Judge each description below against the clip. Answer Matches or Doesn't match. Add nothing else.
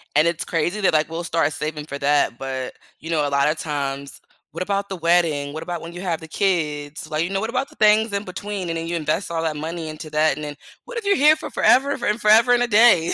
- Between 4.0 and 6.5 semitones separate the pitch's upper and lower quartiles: Matches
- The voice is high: Doesn't match